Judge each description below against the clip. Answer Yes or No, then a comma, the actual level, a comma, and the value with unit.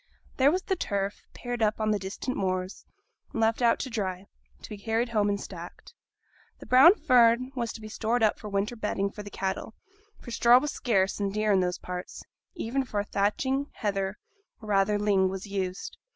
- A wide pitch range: No, average, 3.3 semitones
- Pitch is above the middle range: Yes, high, 210 Hz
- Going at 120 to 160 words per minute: No, average, 195 wpm